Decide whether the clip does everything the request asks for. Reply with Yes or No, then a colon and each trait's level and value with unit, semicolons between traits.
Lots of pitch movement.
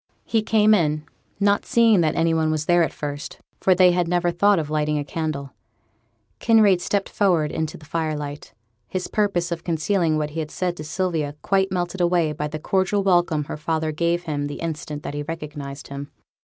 No: average, 3.3 semitones